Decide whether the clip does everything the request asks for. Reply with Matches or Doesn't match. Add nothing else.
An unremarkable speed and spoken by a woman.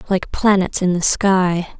Matches